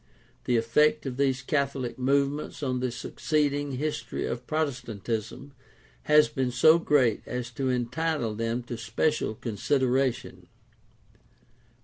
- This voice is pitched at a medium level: No, low, 130 Hz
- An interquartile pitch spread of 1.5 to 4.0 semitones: Yes, average, 3.2 semitones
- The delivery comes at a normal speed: No, slow, 120 wpm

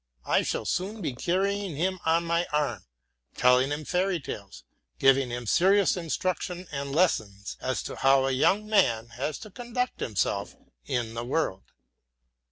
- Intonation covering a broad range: Yes, wide, 6.9 semitones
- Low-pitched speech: No, medium, 150 Hz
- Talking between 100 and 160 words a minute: Yes, average, 155 wpm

